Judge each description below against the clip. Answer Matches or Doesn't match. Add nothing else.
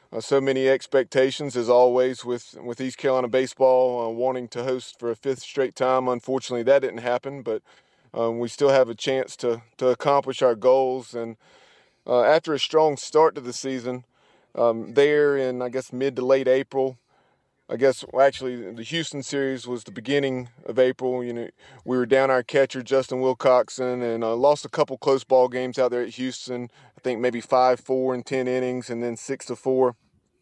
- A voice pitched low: Matches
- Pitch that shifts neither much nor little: Doesn't match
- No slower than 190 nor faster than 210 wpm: Matches